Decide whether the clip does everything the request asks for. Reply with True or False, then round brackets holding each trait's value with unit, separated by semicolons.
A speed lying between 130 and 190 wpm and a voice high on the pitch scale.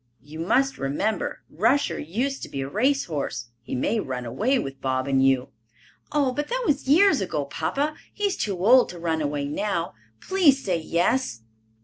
False (185 wpm; 180 Hz)